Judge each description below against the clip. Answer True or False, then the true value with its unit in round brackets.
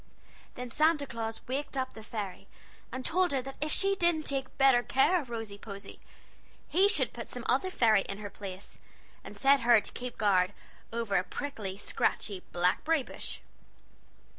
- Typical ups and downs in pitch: False (5.8 semitones)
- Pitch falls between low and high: False (245 Hz)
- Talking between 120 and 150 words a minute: False (170 wpm)